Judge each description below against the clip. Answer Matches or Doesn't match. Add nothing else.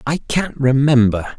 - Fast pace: Doesn't match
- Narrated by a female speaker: Doesn't match